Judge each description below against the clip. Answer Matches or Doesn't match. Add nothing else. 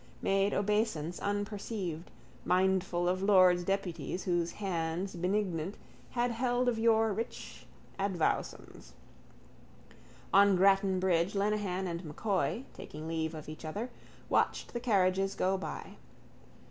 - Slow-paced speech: Matches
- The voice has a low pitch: Doesn't match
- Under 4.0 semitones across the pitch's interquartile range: Matches